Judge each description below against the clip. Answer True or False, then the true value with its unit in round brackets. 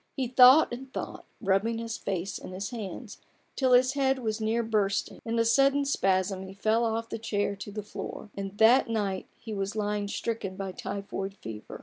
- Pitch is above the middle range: True (215 Hz)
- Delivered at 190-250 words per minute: True (195 wpm)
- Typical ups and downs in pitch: True (3.2 semitones)